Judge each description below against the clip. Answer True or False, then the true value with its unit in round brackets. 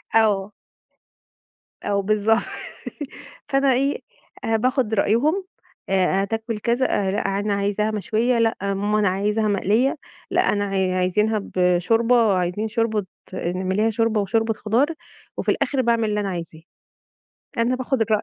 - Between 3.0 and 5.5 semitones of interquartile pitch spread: False (2.6 semitones)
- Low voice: False (215 Hz)